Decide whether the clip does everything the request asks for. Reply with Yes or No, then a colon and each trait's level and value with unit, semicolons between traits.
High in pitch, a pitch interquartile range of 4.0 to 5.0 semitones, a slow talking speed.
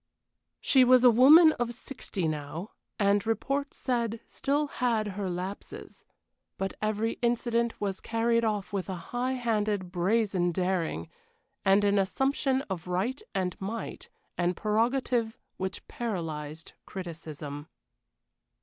Yes: high, 210 Hz; average, 4.6 semitones; slow, 120 wpm